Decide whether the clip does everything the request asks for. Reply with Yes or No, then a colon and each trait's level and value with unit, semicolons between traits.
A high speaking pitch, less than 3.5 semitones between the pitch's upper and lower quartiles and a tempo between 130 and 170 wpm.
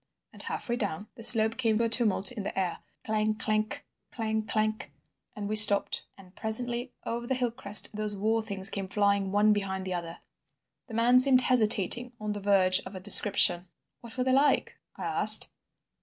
No: high, 215 Hz; average, 2.7 semitones; average, 185 wpm